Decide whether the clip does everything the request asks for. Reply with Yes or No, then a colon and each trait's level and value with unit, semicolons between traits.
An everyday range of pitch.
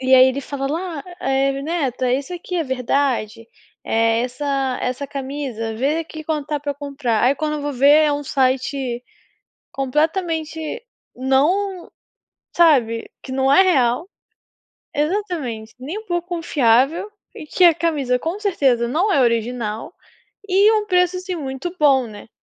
Yes: average, 4.5 semitones